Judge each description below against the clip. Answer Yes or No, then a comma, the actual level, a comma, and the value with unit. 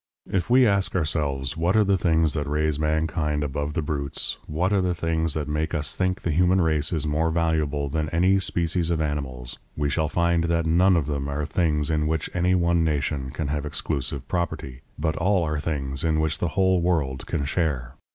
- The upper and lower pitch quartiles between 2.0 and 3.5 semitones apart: Yes, narrow, 2.6 semitones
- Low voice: Yes, very low, 80 Hz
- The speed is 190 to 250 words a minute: Yes, average, 200 wpm